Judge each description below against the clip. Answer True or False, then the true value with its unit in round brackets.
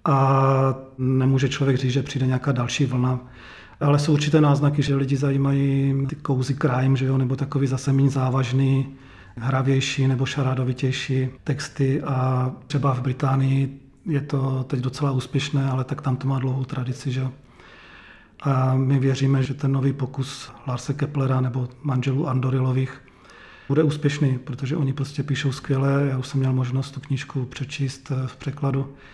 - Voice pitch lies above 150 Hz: False (135 Hz)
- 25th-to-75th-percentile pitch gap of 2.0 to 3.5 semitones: False (1.0 semitones)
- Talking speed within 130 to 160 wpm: True (150 wpm)